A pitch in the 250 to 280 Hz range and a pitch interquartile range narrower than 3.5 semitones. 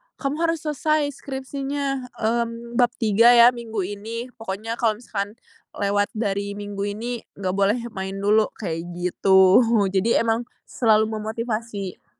No: high, 225 Hz; average, 3.0 semitones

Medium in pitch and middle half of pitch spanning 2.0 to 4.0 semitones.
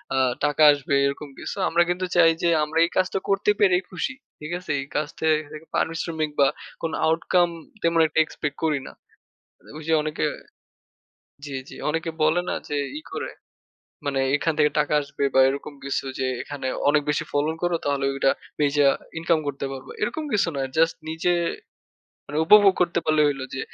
Yes: medium, 155 Hz; average, 2.8 semitones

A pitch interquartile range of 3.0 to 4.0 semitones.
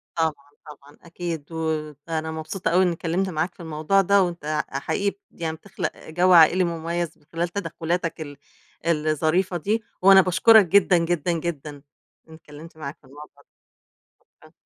No: narrow, 2.5 semitones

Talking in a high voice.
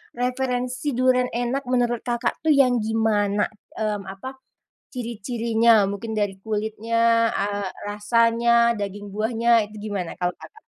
Yes: high, 230 Hz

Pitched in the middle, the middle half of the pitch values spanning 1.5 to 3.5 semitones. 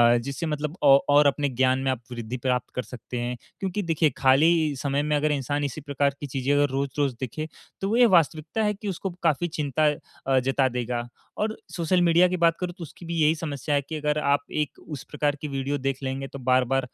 Yes: medium, 145 Hz; average, 3.2 semitones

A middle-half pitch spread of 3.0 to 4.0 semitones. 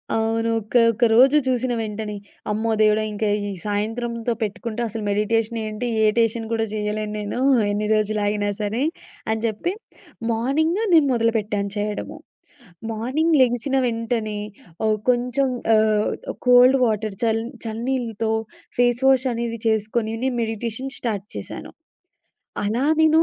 No: narrow, 2.5 semitones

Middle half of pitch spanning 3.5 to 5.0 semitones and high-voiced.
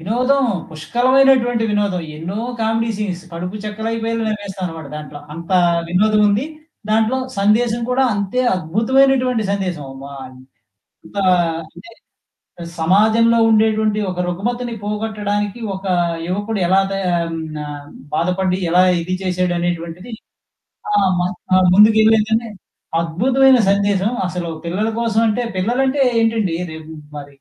Yes: average, 4.2 semitones; high, 205 Hz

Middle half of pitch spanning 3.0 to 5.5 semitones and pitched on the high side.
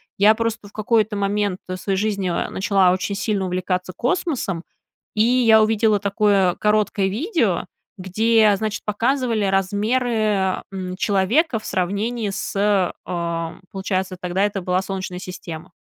No: narrow, 2.6 semitones; high, 200 Hz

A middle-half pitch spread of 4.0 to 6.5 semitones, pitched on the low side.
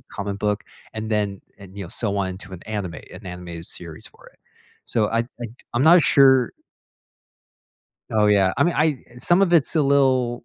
Yes: average, 5.3 semitones; low, 105 Hz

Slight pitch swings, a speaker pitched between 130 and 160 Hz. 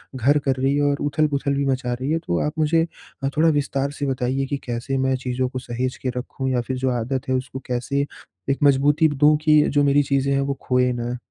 Yes: narrow, 2.0 semitones; low, 135 Hz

